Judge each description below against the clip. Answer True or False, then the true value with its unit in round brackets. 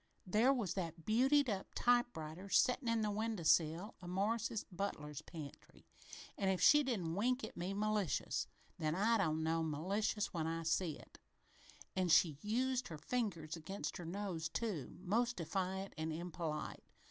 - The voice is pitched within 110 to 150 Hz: False (190 Hz)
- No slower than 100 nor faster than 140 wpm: False (160 wpm)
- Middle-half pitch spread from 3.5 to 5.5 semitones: True (5.2 semitones)